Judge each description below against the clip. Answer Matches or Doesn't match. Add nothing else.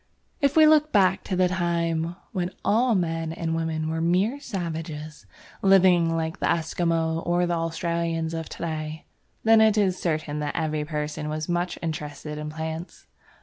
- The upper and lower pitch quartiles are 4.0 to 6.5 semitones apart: Doesn't match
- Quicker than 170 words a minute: Doesn't match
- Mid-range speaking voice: Matches